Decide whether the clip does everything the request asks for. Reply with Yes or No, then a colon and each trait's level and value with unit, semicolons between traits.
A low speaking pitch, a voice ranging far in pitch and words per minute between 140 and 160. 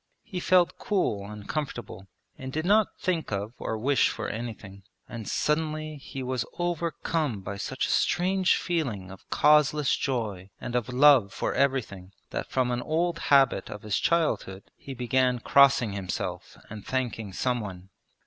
Yes: low, 130 Hz; wide, 6.6 semitones; average, 155 wpm